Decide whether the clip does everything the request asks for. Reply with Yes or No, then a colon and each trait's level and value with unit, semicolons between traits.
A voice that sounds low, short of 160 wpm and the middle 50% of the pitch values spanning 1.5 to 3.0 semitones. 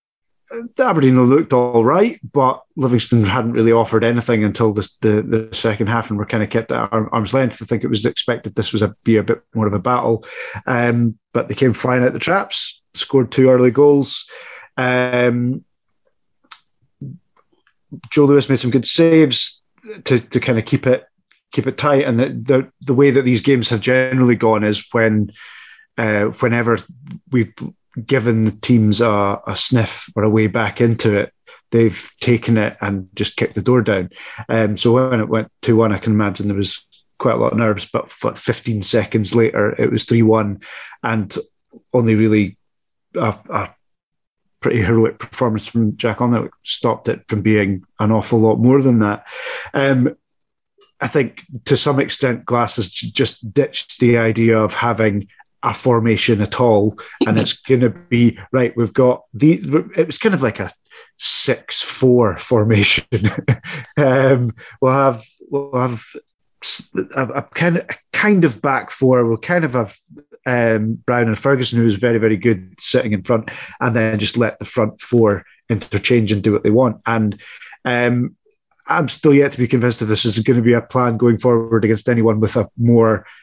No: low, 120 Hz; average, 180 wpm; average, 2.7 semitones